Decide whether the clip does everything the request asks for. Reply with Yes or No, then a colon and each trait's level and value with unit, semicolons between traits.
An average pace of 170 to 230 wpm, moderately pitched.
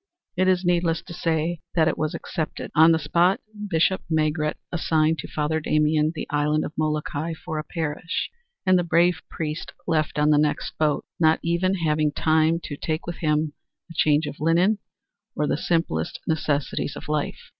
Yes: average, 175 wpm; medium, 160 Hz